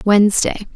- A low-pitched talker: No, high, 205 Hz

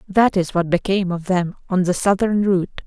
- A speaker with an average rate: No, fast, 210 wpm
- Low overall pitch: No, medium, 185 Hz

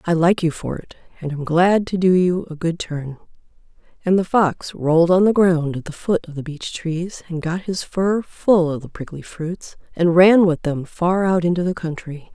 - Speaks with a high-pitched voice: No, medium, 170 Hz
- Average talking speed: No, fast, 225 wpm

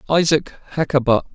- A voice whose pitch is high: No, medium, 145 Hz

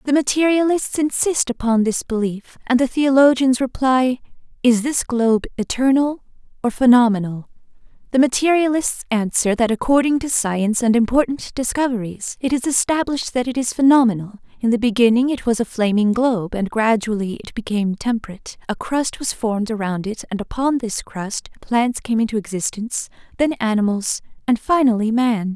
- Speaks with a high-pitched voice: Yes, high, 240 Hz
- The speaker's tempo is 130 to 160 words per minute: Yes, average, 155 wpm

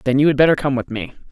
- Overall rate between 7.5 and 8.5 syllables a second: Yes, 7.6 syllables/s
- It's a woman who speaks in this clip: No, male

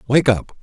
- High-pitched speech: No, low, 130 Hz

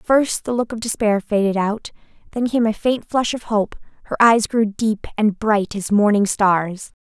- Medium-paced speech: Yes, average, 195 wpm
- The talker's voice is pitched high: Yes, high, 215 Hz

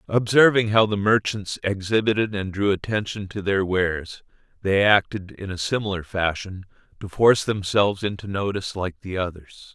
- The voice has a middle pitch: No, low, 100 Hz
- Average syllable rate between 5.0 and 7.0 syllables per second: Yes, 5.1 syllables/s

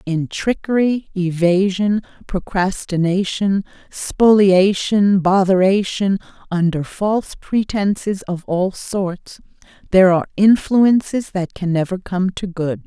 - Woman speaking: Yes, female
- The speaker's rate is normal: No, slow, 100 wpm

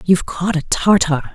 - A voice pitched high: No, medium, 175 Hz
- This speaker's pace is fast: No, average, 180 wpm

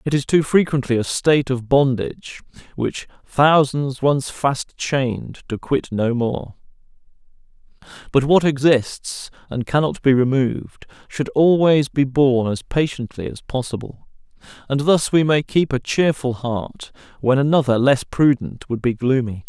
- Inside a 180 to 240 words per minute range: No, average, 145 wpm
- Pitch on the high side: No, low, 135 Hz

